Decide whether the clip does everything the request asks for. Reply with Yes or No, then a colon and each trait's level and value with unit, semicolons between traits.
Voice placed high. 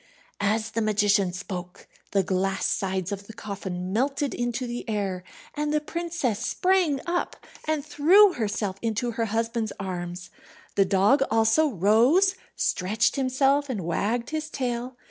Yes: high, 225 Hz